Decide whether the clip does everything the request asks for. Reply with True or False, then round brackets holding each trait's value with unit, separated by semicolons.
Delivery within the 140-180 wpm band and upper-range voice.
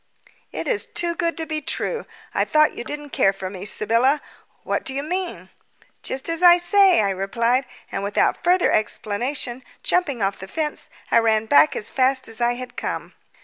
False (190 wpm; 260 Hz)